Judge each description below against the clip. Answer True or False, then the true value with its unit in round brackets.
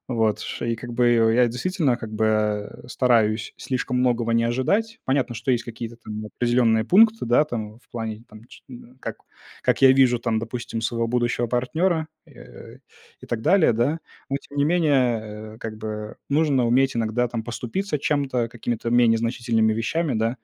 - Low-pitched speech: True (120 Hz)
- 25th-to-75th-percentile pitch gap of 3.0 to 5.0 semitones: False (2.6 semitones)